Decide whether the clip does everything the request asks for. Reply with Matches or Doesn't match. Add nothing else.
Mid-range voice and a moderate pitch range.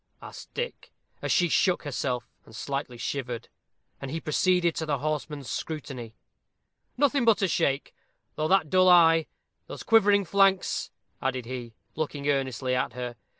Doesn't match